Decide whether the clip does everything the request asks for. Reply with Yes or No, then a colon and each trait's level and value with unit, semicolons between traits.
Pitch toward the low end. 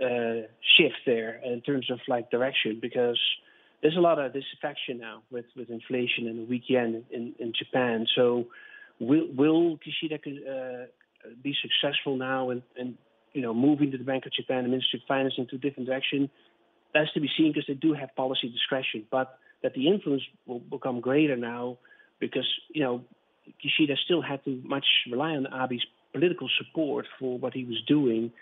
Yes: low, 130 Hz